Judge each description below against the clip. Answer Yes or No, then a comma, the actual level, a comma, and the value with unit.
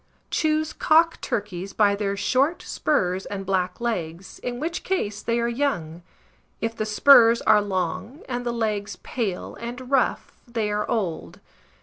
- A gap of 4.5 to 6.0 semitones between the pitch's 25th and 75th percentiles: No, average, 4.1 semitones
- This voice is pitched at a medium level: No, high, 220 Hz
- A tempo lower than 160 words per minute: Yes, average, 150 wpm